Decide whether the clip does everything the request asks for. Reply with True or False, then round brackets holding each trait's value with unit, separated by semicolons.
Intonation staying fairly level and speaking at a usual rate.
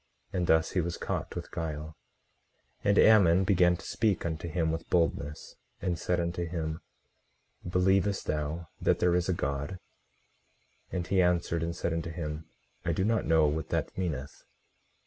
True (2.2 semitones; 170 wpm)